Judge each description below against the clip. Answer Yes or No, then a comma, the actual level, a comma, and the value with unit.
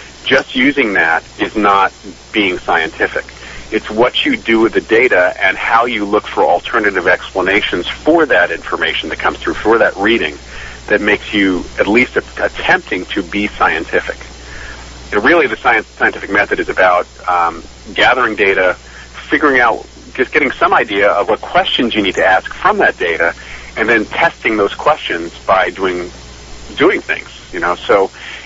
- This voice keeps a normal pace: Yes, average, 165 wpm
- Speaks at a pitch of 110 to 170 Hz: No, very low, 70 Hz